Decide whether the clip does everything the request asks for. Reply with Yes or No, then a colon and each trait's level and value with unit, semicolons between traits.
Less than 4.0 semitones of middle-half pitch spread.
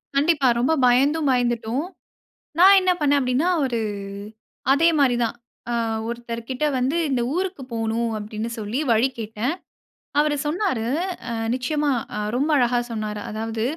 No: average, 4.3 semitones